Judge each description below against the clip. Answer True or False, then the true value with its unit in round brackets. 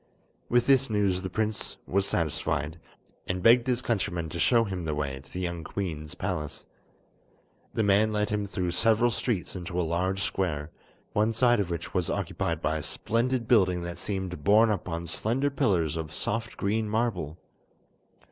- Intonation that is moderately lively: True (4.7 semitones)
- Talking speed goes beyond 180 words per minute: False (175 wpm)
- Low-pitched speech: True (95 Hz)